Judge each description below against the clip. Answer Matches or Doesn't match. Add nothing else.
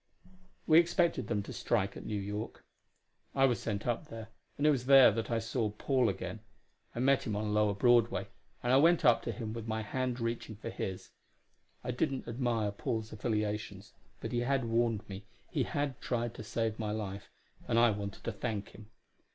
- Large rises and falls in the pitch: Doesn't match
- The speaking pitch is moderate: Doesn't match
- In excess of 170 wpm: Matches